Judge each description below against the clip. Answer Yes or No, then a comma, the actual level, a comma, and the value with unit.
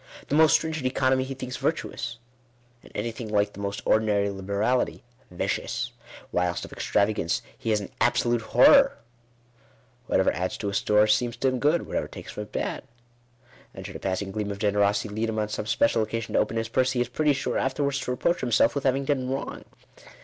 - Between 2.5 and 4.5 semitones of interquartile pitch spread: Yes, average, 4.2 semitones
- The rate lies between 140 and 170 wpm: No, average, 200 wpm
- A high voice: No, low, 115 Hz